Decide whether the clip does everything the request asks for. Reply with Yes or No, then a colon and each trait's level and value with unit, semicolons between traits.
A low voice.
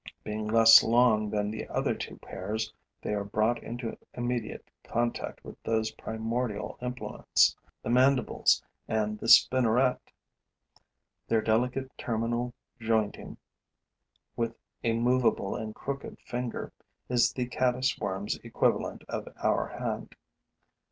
Yes: low, 115 Hz